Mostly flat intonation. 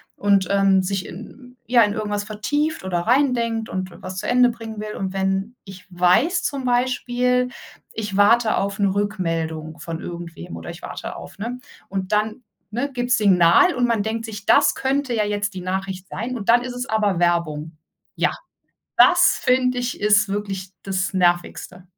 No: average, 4.6 semitones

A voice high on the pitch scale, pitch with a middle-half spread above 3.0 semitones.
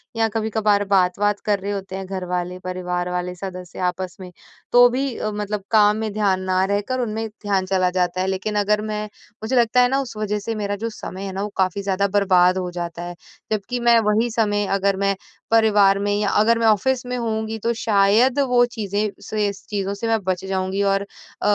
No: high, 200 Hz; narrow, 2.6 semitones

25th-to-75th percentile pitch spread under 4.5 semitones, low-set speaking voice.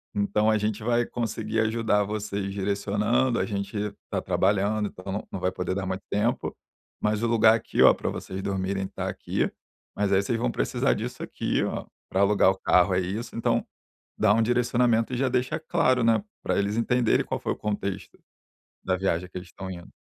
Yes: average, 2.9 semitones; low, 105 Hz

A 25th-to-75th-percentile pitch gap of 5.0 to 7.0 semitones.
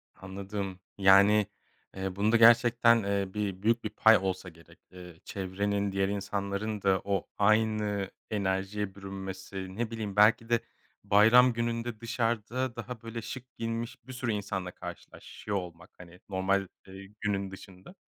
No: average, 3.0 semitones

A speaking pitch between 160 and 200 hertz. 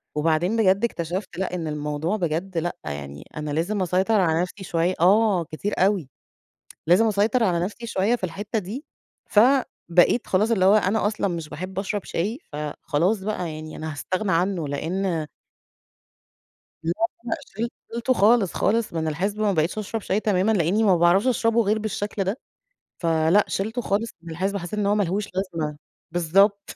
Yes: high, 190 Hz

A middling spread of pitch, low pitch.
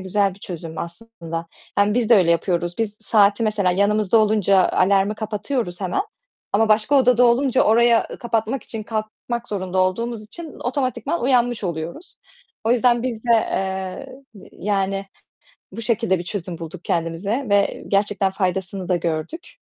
No: average, 3.9 semitones; high, 210 Hz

